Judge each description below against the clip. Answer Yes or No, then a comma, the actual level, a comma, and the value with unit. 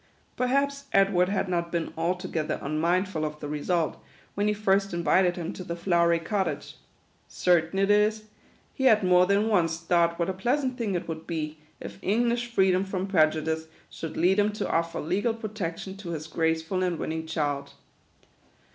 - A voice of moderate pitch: Yes, medium, 180 Hz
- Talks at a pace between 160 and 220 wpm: Yes, average, 175 wpm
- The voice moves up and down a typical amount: Yes, average, 3.6 semitones